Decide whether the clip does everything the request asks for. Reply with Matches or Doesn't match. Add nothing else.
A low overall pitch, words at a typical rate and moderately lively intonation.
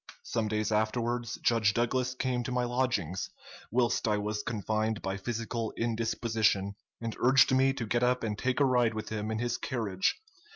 Doesn't match